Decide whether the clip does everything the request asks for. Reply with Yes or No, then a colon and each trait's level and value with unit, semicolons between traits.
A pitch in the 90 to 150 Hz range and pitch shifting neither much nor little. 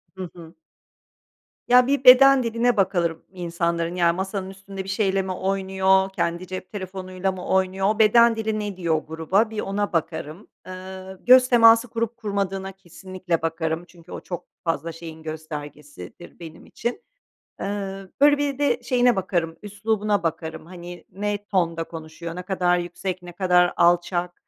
No: medium, 185 Hz; average, 3.3 semitones